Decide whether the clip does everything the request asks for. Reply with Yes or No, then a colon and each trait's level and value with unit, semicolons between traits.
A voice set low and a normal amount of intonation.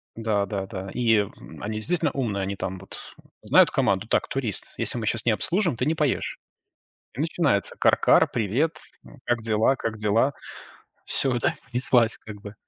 Yes: low, 115 Hz; average, 4.0 semitones